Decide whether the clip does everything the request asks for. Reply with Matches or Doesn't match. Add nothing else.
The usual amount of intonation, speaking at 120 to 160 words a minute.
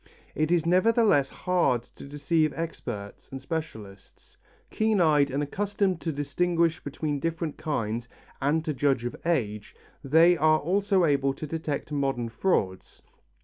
Matches